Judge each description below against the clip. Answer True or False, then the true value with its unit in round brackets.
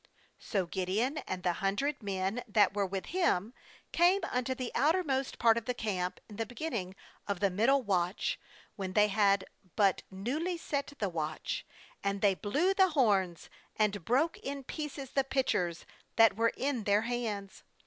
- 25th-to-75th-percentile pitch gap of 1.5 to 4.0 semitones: False (5.6 semitones)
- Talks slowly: False (165 wpm)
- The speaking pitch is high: True (215 Hz)